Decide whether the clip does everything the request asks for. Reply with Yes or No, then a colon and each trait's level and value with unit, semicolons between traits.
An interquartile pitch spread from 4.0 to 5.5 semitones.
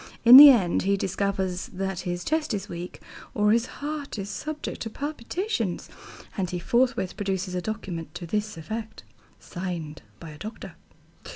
Yes: average, 4.5 semitones